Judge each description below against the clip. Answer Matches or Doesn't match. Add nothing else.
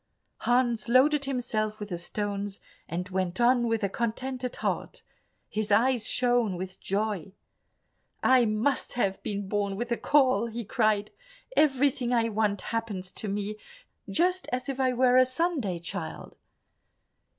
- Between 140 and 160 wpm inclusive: Matches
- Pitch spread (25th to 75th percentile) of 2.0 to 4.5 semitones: Matches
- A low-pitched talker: Doesn't match